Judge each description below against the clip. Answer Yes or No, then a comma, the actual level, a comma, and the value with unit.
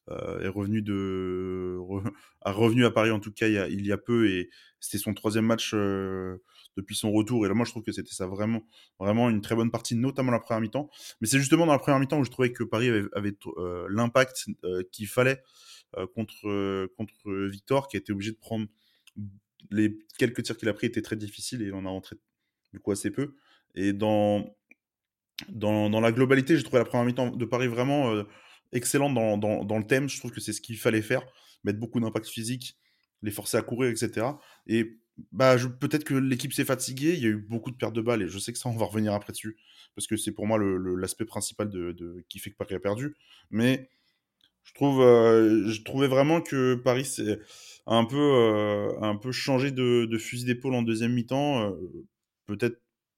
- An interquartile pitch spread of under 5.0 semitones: Yes, average, 3.1 semitones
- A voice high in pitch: No, low, 110 Hz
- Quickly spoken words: Yes, fast, 225 wpm